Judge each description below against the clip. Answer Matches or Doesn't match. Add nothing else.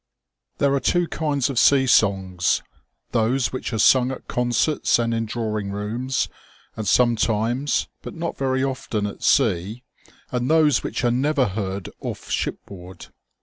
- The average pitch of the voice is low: Matches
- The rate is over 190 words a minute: Doesn't match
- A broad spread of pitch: Doesn't match